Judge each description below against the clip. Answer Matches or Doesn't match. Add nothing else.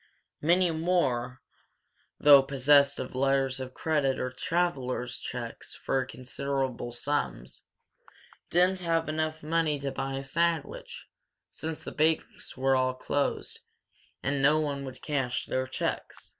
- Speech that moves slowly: Matches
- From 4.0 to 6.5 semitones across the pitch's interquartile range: Doesn't match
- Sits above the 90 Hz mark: Matches